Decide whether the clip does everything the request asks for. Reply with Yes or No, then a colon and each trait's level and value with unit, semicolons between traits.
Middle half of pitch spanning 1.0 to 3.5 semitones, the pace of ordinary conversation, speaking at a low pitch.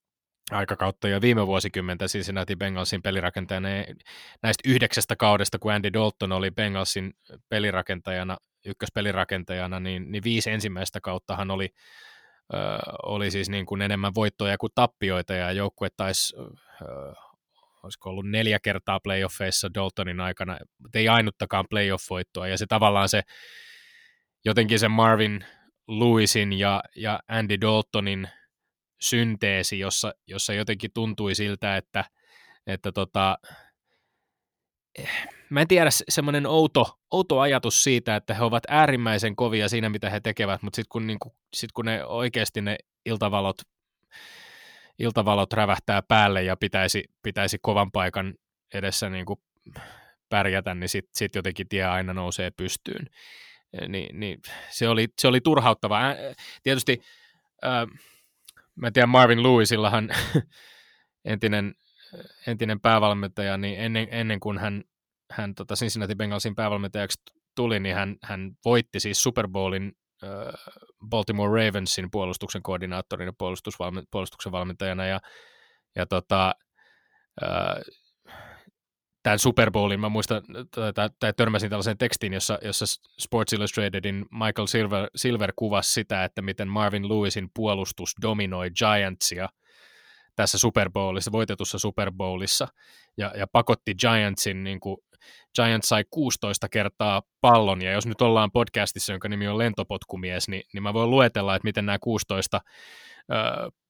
Yes: narrow, 2.6 semitones; average, 125 wpm; low, 105 Hz